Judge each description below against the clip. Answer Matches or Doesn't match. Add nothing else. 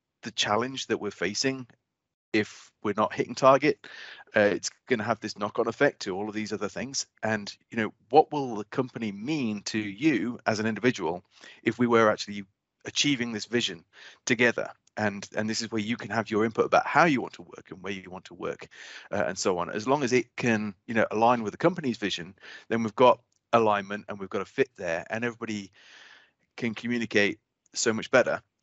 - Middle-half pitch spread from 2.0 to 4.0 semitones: Matches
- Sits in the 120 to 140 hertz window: Doesn't match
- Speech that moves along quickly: Matches